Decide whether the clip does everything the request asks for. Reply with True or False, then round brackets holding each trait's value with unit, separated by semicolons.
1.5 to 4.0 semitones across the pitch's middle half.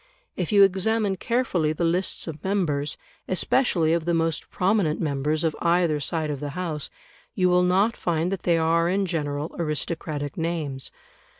True (3.1 semitones)